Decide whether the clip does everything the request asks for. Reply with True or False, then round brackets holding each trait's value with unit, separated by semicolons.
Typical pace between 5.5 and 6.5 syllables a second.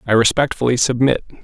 True (6.3 syllables/s)